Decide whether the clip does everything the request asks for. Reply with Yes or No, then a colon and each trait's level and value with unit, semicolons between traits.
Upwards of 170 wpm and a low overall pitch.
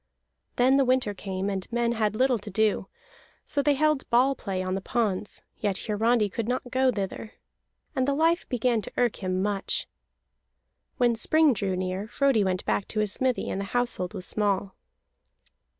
No: average, 180 wpm; high, 220 Hz